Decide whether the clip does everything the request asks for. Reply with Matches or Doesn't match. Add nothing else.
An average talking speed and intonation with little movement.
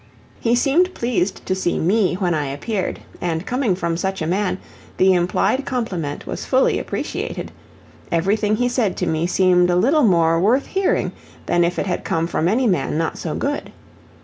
Doesn't match